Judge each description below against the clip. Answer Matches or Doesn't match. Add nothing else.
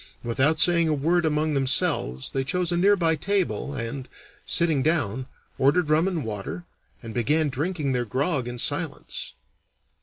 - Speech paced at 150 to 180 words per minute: Matches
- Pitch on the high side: Doesn't match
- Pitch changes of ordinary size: Matches